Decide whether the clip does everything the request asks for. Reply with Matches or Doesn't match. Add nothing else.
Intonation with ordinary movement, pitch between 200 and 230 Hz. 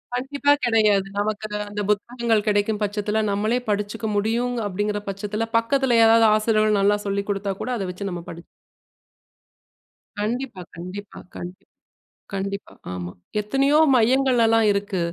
Doesn't match